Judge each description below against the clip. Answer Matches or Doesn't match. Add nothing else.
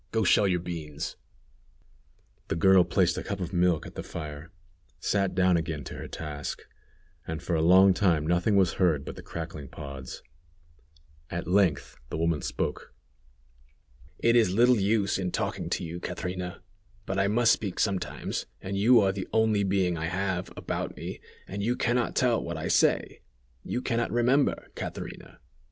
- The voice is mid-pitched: Doesn't match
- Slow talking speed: Doesn't match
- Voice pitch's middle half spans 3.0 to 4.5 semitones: Matches